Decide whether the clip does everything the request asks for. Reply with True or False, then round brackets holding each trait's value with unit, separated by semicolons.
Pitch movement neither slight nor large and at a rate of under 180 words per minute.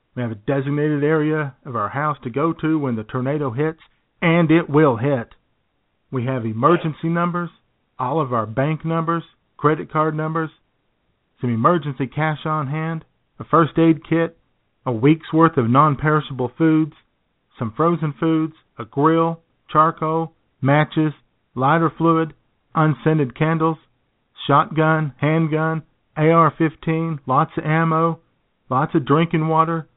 True (3.0 semitones; 140 wpm)